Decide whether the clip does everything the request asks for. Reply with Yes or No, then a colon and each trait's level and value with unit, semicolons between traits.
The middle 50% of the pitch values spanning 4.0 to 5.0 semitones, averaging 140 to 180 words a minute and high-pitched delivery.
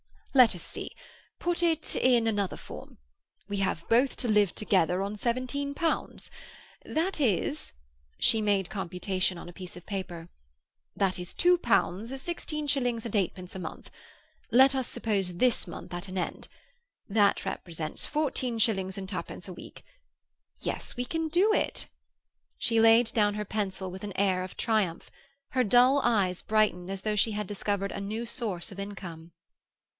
Yes: average, 4.7 semitones; average, 160 wpm; high, 205 Hz